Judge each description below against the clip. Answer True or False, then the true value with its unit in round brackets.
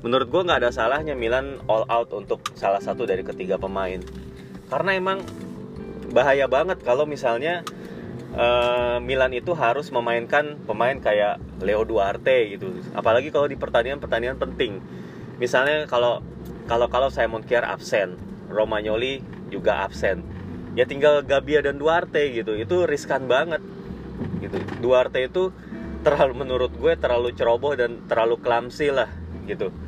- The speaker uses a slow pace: False (135 wpm)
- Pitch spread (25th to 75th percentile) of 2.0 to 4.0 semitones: False (5.5 semitones)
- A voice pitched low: True (120 Hz)